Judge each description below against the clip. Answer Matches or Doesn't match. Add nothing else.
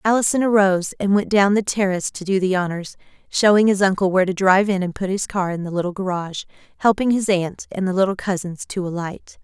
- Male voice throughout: Doesn't match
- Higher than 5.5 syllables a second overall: Matches